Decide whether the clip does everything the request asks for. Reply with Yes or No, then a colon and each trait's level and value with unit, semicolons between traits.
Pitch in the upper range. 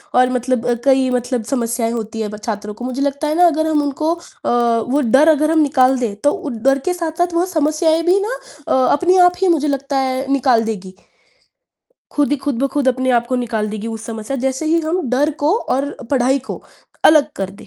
Yes: very high, 270 Hz